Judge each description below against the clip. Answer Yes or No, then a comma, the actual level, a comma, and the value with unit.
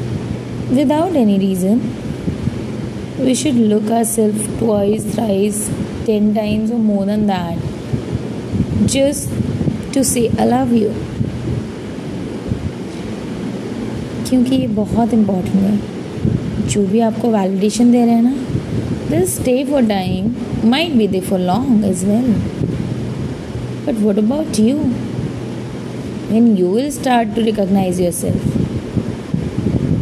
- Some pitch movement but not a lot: Yes, average, 3.4 semitones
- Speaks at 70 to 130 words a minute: Yes, average, 115 wpm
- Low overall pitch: No, high, 220 Hz